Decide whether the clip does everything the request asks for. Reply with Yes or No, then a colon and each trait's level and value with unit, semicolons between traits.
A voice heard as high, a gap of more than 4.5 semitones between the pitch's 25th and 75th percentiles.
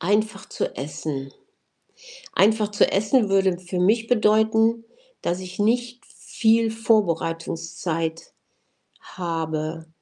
Yes: high, 195 Hz; average, 5.0 semitones